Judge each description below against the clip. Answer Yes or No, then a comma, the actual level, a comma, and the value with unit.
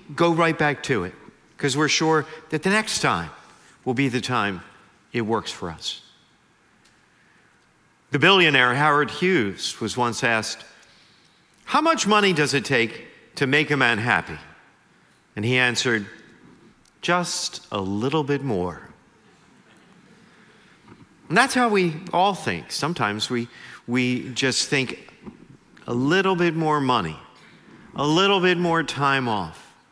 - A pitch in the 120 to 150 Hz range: Yes, medium, 140 Hz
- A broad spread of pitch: Yes, wide, 6.9 semitones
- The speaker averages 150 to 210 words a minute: No, slow, 135 wpm